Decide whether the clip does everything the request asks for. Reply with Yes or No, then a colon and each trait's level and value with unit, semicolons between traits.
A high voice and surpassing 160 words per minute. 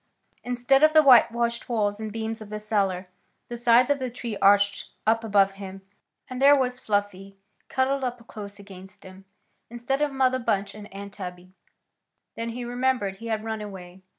Yes: high, 220 Hz; average, 180 wpm